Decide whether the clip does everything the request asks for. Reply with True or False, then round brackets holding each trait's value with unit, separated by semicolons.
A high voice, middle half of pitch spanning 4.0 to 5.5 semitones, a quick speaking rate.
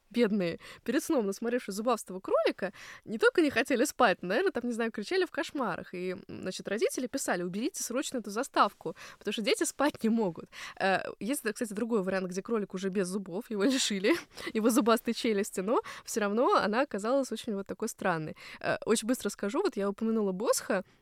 True (225 Hz; 4.5 semitones; 180 wpm)